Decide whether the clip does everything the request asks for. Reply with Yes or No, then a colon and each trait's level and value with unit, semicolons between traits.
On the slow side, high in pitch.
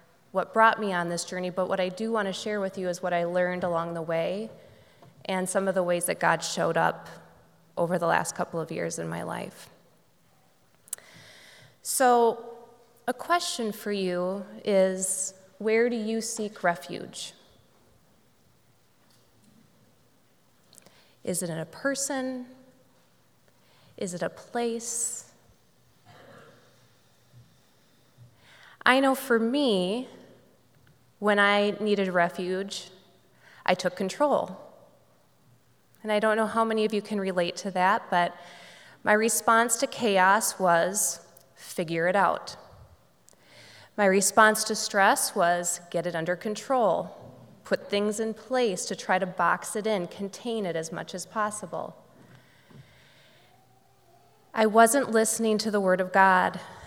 Yes: slow, 130 wpm; high, 195 Hz